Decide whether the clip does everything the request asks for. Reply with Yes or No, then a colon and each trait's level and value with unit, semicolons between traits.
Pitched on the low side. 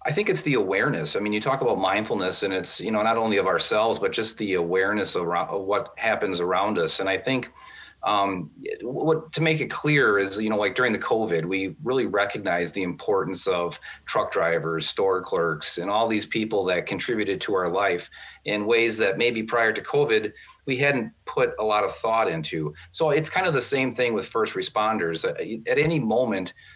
Yes: low, 125 Hz